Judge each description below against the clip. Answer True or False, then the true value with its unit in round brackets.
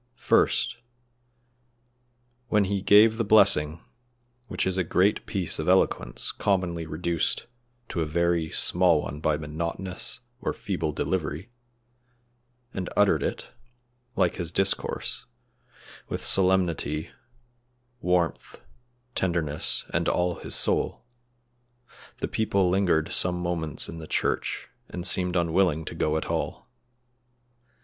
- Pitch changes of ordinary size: True (3.0 semitones)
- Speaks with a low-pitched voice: True (90 Hz)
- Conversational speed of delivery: False (115 wpm)